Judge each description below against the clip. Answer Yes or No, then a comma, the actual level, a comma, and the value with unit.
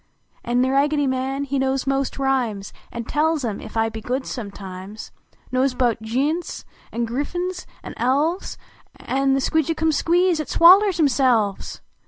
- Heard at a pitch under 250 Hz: No, very high, 270 Hz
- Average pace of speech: Yes, average, 150 wpm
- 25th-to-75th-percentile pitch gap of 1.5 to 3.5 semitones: No, average, 4.4 semitones